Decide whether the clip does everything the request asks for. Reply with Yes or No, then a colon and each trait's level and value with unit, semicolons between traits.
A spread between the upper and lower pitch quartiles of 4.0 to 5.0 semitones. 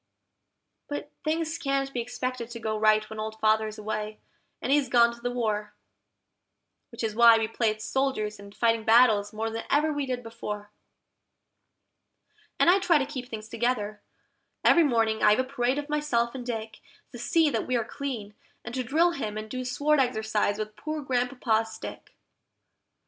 No: average, 3.6 semitones